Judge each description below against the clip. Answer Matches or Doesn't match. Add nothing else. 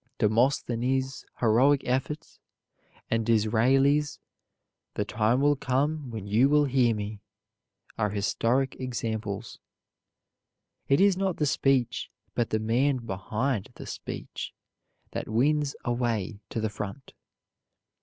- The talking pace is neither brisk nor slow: Doesn't match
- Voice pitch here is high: Doesn't match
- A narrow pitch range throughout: Doesn't match